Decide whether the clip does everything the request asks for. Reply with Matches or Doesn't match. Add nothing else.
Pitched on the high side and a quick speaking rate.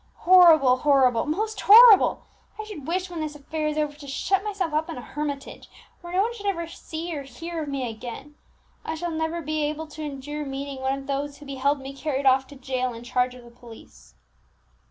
Matches